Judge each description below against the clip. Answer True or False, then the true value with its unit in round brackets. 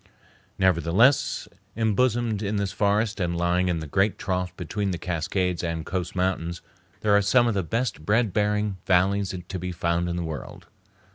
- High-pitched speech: False (95 Hz)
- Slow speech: False (170 wpm)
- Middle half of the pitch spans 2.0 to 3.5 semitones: True (3.1 semitones)